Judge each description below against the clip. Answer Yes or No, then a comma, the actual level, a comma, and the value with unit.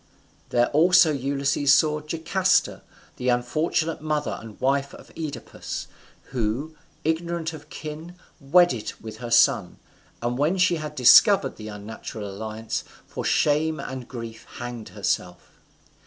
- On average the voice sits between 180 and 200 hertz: No, medium, 140 Hz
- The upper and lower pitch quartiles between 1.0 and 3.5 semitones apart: No, average, 5.0 semitones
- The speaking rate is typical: No, slow, 125 wpm